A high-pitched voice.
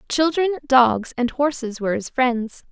Yes: very high, 260 Hz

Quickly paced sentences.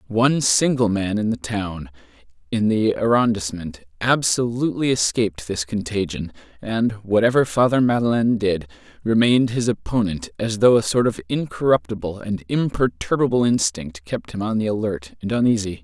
No: average, 140 wpm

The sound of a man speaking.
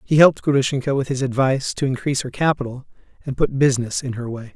Yes: male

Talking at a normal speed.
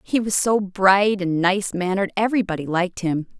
Yes: average, 175 wpm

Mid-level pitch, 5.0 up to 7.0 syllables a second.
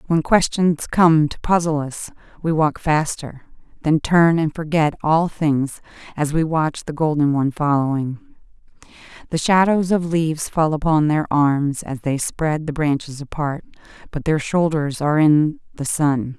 No: medium, 155 Hz; 4.3 syllables/s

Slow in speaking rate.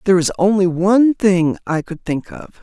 No: fast, 205 wpm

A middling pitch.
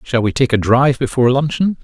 No: low, 130 Hz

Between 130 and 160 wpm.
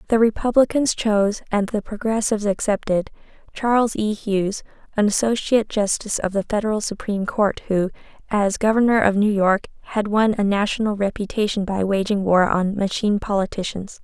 Yes: average, 150 wpm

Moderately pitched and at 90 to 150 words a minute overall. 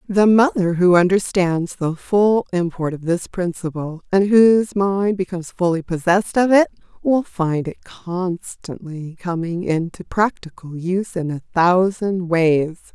Yes: medium, 180 Hz; average, 140 wpm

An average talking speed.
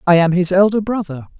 No: fast, 215 wpm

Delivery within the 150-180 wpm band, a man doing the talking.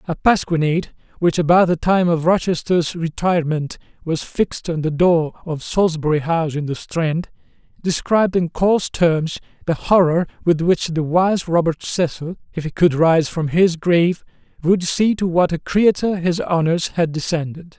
Yes: average, 165 wpm; male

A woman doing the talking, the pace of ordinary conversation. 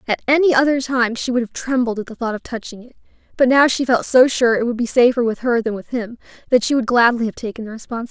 No: female; fast, 275 wpm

